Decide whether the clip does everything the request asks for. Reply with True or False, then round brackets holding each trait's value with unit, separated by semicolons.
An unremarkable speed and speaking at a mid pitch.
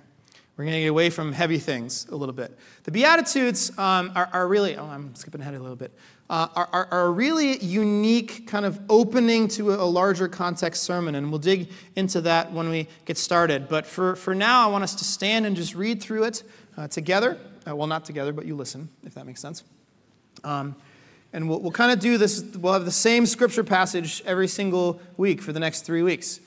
False (220 wpm; 180 Hz)